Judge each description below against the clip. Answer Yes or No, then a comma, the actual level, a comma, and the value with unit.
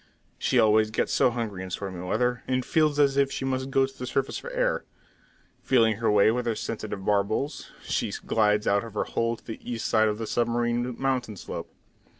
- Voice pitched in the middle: No, low, 115 Hz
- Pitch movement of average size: Yes, average, 3.5 semitones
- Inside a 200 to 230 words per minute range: Yes, fast, 205 wpm